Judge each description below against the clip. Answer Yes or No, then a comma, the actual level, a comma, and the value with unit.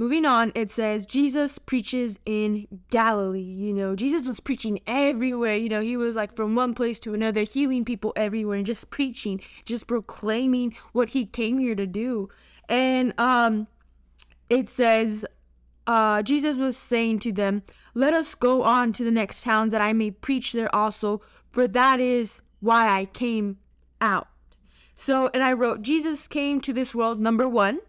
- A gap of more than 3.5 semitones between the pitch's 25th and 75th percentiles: No, average, 3.1 semitones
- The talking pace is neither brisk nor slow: Yes, average, 170 wpm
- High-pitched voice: Yes, high, 230 Hz